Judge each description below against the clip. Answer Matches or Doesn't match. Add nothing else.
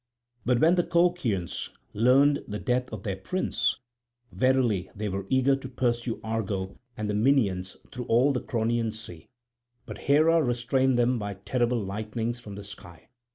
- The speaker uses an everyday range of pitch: Matches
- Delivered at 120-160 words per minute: Matches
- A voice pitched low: Matches